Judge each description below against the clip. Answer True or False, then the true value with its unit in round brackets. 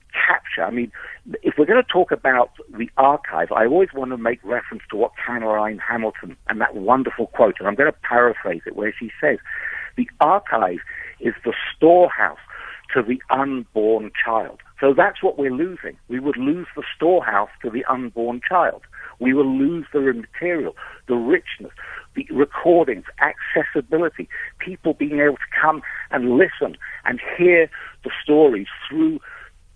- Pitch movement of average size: False (6.7 semitones)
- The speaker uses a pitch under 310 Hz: True (140 Hz)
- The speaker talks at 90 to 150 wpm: False (160 wpm)